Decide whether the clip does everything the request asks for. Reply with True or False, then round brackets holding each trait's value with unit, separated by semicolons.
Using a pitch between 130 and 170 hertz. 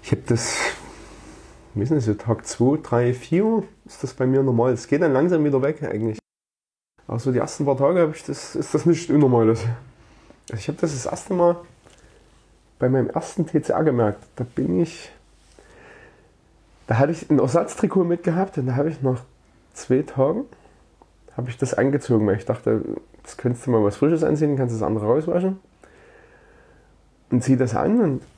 True (135 Hz)